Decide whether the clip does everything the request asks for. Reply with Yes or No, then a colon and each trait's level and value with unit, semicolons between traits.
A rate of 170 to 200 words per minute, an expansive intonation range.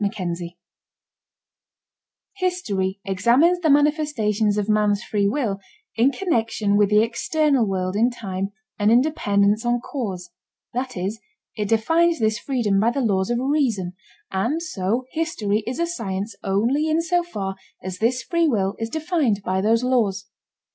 No: average, 155 wpm; wide, 5.9 semitones